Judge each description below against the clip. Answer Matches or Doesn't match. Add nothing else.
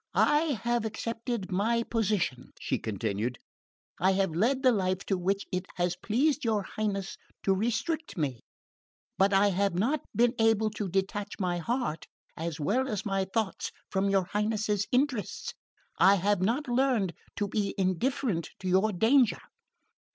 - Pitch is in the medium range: Doesn't match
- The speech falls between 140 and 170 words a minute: Matches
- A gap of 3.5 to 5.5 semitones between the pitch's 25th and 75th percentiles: Matches